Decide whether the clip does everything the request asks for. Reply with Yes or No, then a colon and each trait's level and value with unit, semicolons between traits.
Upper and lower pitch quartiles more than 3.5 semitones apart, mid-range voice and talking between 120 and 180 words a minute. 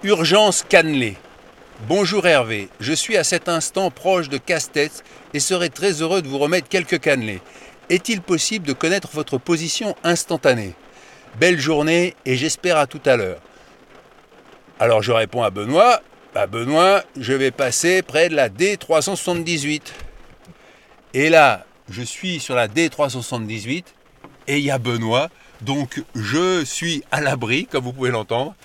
Yes: average, 5.1 semitones; medium, 160 Hz; average, 150 wpm